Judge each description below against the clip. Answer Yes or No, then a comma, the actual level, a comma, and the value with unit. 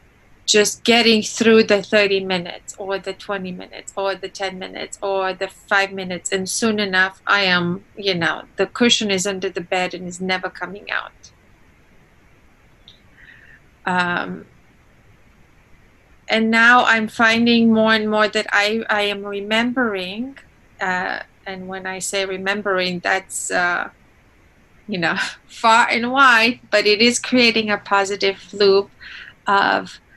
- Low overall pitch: No, high, 200 Hz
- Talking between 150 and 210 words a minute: No, average, 140 wpm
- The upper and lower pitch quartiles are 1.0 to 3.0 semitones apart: Yes, average, 2.7 semitones